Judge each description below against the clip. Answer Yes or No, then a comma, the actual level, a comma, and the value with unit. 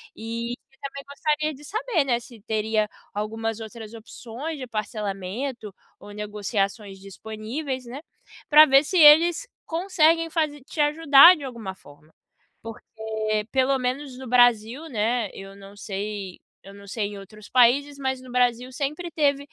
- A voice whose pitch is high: Yes, high, 245 Hz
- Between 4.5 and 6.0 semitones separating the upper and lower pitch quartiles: Yes, average, 5.1 semitones